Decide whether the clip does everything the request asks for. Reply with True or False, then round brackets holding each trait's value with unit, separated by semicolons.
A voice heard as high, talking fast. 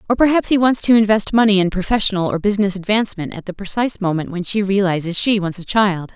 True (200 Hz; 225 wpm)